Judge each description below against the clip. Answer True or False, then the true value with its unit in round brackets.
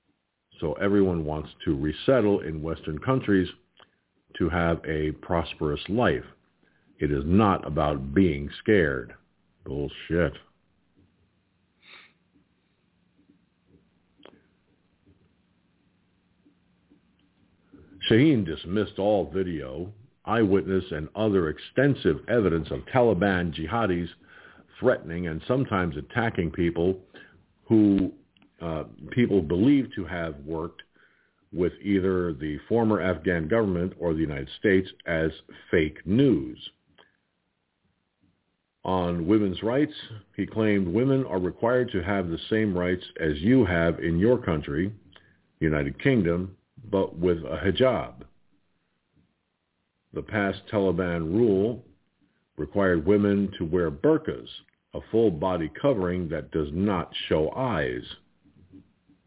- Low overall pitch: True (95 Hz)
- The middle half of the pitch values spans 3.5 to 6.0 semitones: True (4.1 semitones)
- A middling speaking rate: False (100 wpm)